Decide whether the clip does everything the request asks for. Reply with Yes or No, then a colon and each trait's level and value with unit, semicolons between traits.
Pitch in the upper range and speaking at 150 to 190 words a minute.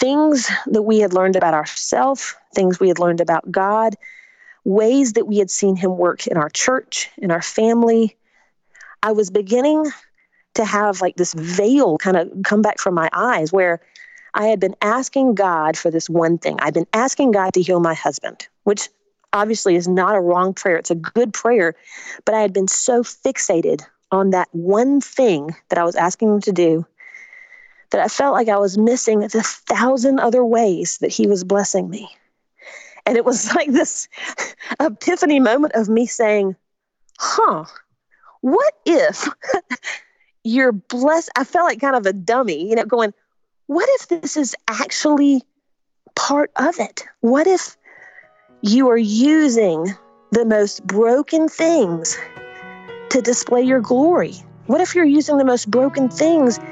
Yes: high, 225 Hz; average, 165 wpm